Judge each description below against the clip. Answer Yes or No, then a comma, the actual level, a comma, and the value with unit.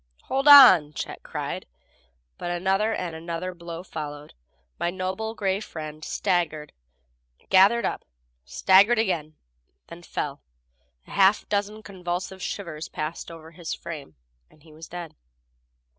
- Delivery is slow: Yes, slow, 130 wpm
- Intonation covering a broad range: No, average, 3.6 semitones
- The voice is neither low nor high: Yes, medium, 175 Hz